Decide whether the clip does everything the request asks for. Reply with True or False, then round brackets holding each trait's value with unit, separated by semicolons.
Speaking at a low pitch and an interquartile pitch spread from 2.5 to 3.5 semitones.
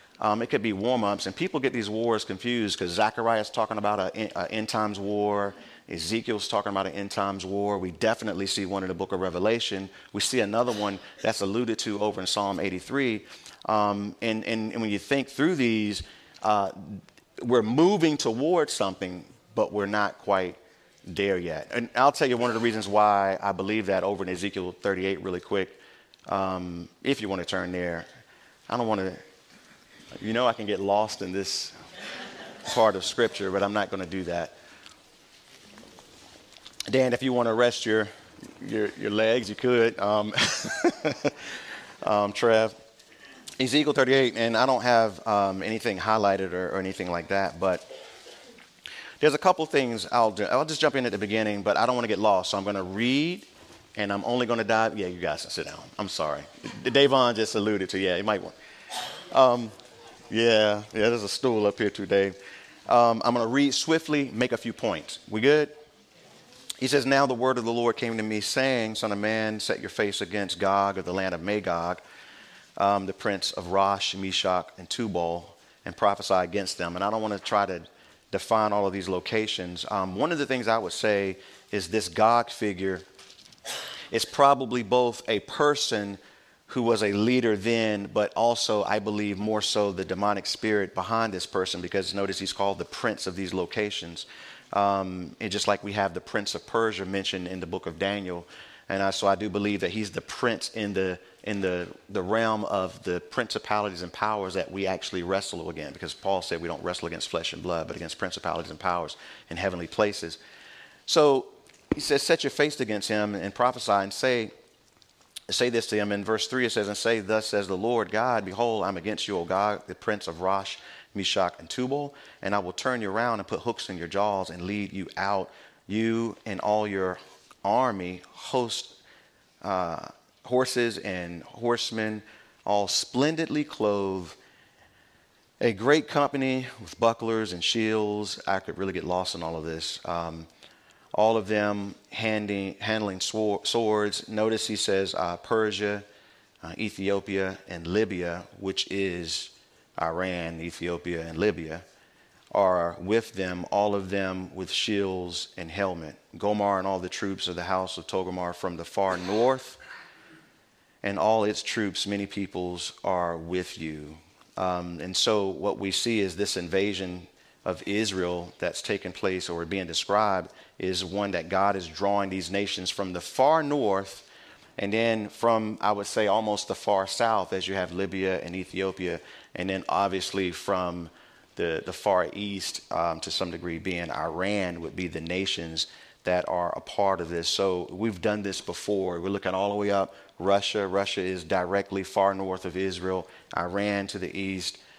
True (100 Hz; 2.8 semitones)